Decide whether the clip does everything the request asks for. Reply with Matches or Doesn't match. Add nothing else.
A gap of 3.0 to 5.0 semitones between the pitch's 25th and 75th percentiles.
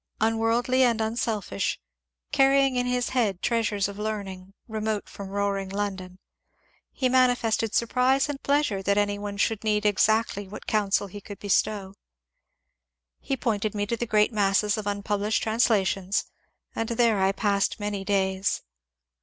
Doesn't match